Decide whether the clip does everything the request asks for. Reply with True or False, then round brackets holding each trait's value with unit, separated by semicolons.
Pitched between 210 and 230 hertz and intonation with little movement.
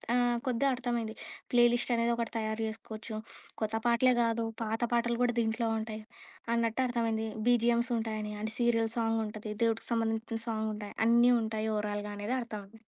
True (225 Hz; 1.5 semitones)